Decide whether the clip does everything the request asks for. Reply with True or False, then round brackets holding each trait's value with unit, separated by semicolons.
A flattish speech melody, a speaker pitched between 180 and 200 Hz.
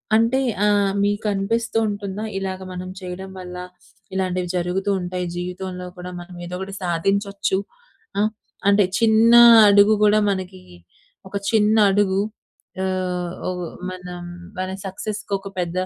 True (2.1 semitones; 190 Hz)